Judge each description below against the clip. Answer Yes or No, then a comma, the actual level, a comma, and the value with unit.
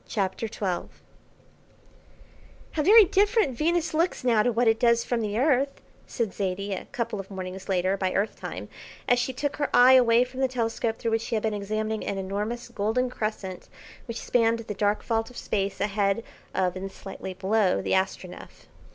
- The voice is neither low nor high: No, high, 225 Hz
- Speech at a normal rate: Yes, average, 185 wpm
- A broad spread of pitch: No, average, 3.9 semitones